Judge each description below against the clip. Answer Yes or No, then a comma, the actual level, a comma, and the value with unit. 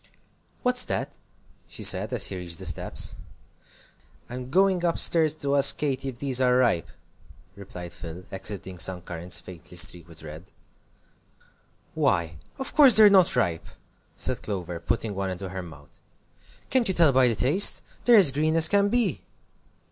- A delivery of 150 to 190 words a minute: Yes, average, 165 wpm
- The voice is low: Yes, low, 120 Hz